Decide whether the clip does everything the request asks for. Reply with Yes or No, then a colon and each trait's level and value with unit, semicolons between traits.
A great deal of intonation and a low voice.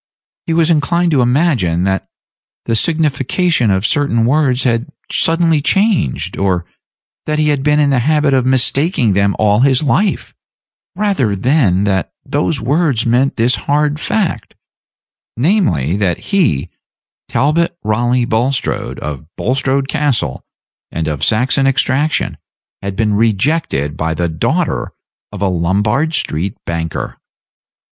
Yes: wide, 7.2 semitones; low, 125 Hz